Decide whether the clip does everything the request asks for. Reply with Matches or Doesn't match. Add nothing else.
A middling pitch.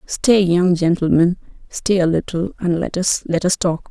Matches